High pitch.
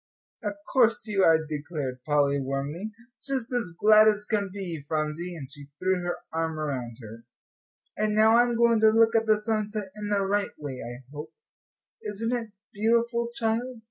Yes: high, 205 Hz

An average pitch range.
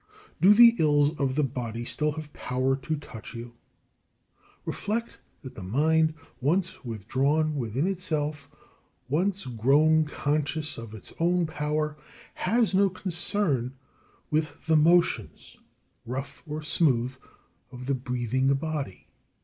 Yes: average, 3.7 semitones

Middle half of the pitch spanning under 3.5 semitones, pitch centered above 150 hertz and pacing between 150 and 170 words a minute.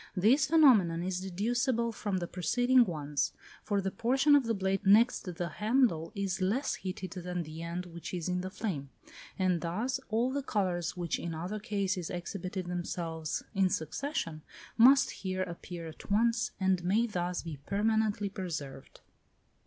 No: average, 4.2 semitones; high, 190 Hz; average, 160 wpm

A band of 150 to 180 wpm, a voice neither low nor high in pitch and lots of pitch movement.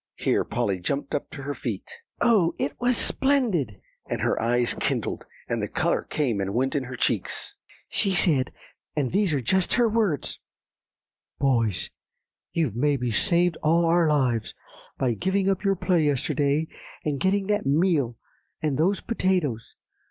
Yes: average, 160 wpm; medium, 150 Hz; wide, 6.6 semitones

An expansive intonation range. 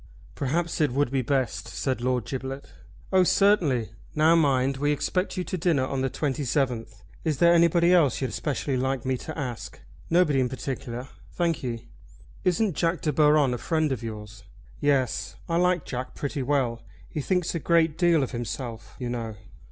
No: average, 4.7 semitones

